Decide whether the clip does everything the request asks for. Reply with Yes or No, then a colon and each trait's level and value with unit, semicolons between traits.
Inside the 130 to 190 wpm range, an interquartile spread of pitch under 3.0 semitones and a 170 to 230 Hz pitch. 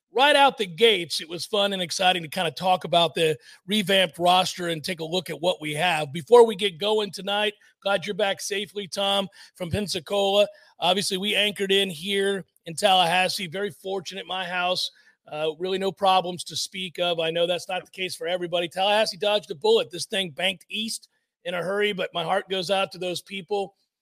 No: fast, 205 wpm; narrow, 2.4 semitones; high, 190 Hz